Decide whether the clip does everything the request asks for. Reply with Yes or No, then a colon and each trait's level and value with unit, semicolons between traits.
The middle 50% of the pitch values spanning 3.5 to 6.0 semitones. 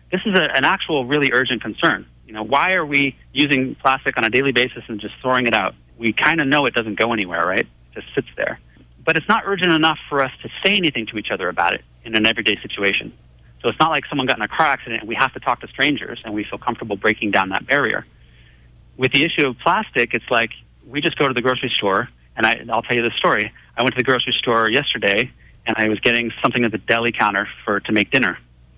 Yes: average, 4.2 semitones